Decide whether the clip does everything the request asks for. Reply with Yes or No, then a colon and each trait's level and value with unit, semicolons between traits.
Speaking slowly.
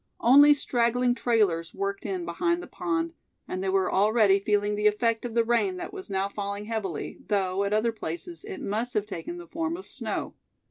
No: average, 195 wpm